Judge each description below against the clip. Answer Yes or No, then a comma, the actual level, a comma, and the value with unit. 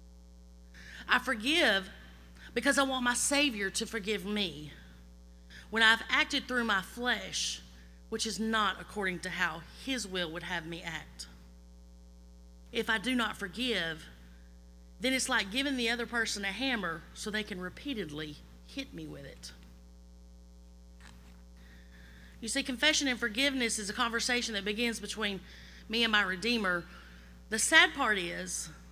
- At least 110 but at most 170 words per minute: Yes, average, 145 wpm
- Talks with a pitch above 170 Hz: Yes, high, 190 Hz